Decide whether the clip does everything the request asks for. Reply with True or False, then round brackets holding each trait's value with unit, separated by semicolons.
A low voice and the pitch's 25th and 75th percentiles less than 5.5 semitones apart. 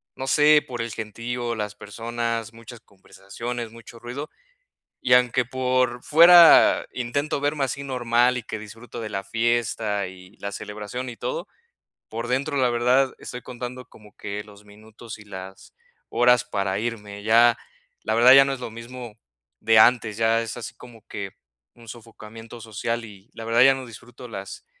True (115 Hz; 2.5 semitones)